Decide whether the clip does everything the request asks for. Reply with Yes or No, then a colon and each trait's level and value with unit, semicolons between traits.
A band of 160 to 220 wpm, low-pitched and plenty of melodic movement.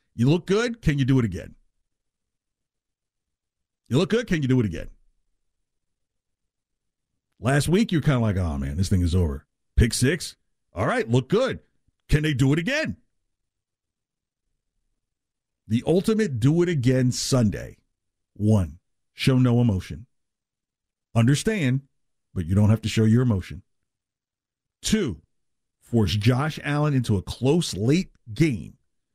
No: average, 140 wpm; low, 125 Hz; wide, 5.8 semitones